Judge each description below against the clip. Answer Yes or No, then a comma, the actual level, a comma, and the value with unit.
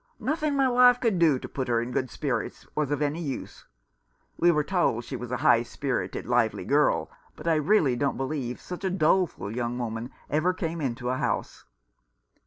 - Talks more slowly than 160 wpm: No, average, 195 wpm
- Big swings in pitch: Yes, wide, 6.0 semitones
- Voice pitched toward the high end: No, medium, 145 Hz